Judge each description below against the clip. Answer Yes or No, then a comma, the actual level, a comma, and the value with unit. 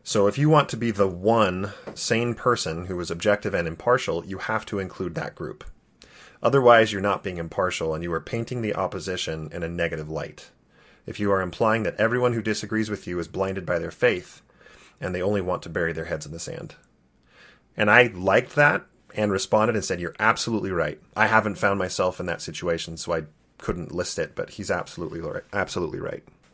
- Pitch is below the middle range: Yes, low, 100 Hz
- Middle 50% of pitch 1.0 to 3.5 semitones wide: No, average, 4.0 semitones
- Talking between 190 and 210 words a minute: Yes, fast, 205 wpm